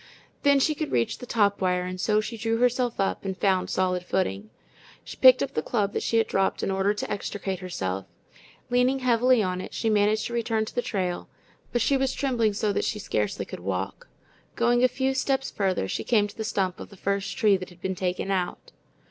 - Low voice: No, high, 205 Hz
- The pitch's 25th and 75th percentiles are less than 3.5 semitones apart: No, average, 4.5 semitones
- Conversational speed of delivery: No, fast, 225 wpm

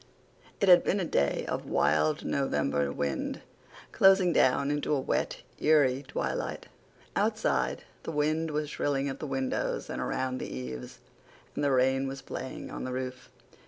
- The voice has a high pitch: No, low, 135 Hz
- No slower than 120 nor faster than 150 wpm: No, average, 160 wpm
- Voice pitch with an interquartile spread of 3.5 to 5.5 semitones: No, average, 2.9 semitones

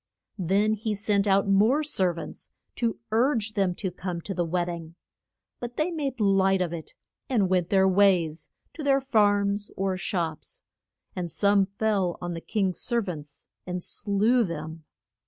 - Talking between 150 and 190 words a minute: Yes, average, 165 wpm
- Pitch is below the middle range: No, high, 195 Hz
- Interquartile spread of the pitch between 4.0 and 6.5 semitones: No, average, 3.5 semitones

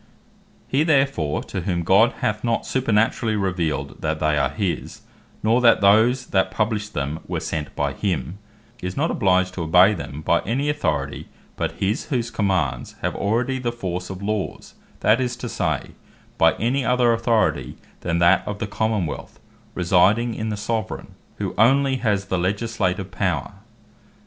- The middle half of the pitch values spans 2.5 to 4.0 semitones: No, average, 4.5 semitones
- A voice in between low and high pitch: No, low, 100 Hz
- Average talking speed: Yes, average, 165 wpm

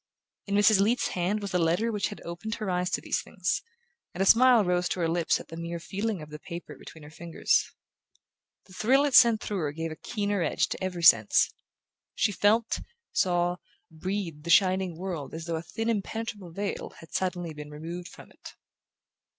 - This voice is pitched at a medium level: Yes, medium, 180 Hz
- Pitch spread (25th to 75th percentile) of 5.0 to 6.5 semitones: No, average, 3.6 semitones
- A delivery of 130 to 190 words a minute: No, average, 200 wpm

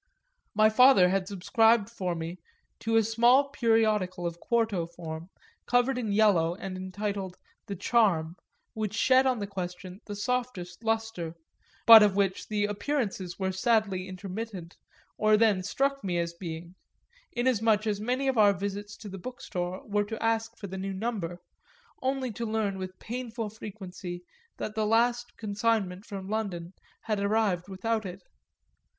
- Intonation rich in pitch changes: No, average, 3.4 semitones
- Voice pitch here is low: No, high, 205 Hz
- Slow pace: No, average, 155 wpm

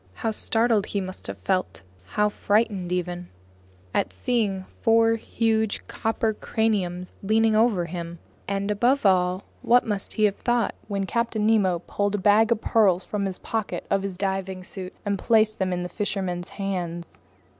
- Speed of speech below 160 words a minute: No, average, 165 wpm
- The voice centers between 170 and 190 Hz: No, high, 200 Hz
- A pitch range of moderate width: Yes, average, 3.1 semitones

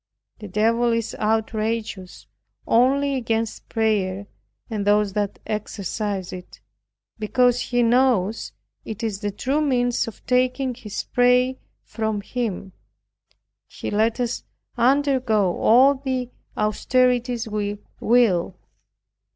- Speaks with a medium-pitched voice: No, high, 225 Hz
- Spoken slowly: Yes, slow, 110 wpm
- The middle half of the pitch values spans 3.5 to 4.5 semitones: No, average, 3.1 semitones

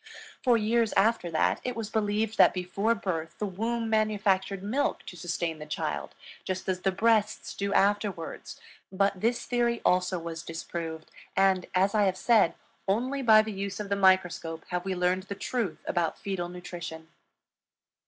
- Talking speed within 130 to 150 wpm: No, average, 165 wpm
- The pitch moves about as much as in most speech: Yes, average, 3.5 semitones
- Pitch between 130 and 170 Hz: No, high, 195 Hz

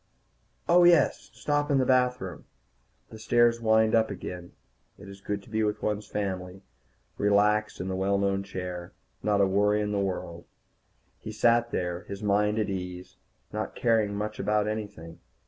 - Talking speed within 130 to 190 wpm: Yes, average, 165 wpm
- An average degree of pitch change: No, narrow, 2.3 semitones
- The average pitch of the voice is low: Yes, low, 105 Hz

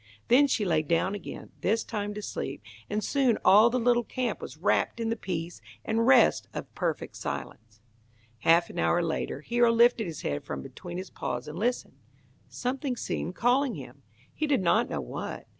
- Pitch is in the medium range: No, high, 215 Hz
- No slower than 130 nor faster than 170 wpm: No, average, 185 wpm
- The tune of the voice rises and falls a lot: Yes, wide, 5.9 semitones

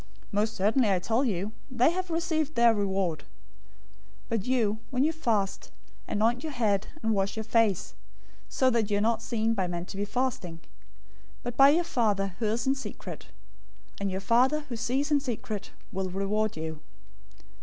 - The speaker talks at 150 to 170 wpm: No, average, 180 wpm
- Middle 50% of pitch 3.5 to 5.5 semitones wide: Yes, average, 4.4 semitones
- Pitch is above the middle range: Yes, high, 225 Hz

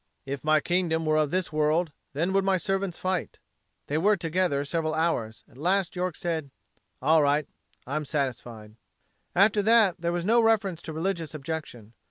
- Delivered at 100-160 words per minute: No, average, 170 wpm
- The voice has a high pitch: No, medium, 165 Hz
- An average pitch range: Yes, average, 3.7 semitones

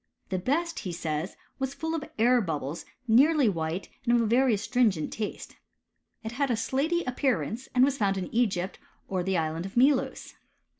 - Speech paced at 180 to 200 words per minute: Yes, average, 185 wpm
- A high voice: Yes, high, 230 Hz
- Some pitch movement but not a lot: No, wide, 6.1 semitones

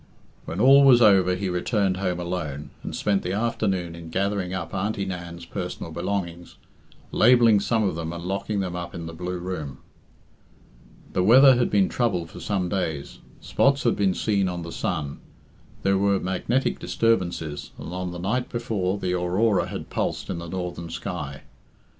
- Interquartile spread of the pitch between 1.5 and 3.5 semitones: Yes, average, 3.0 semitones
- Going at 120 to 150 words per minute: No, average, 170 wpm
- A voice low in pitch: Yes, very low, 95 Hz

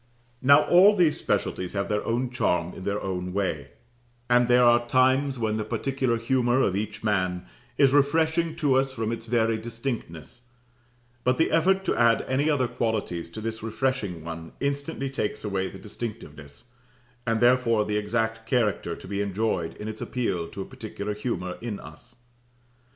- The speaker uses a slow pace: No, average, 170 wpm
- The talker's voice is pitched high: No, low, 115 Hz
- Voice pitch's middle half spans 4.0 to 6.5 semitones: Yes, average, 4.4 semitones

